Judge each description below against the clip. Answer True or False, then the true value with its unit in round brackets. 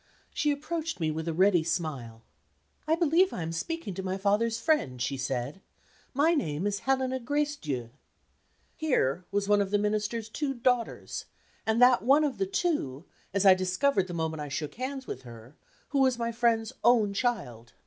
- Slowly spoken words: False (180 wpm)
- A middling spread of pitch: False (8.7 semitones)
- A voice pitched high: True (210 Hz)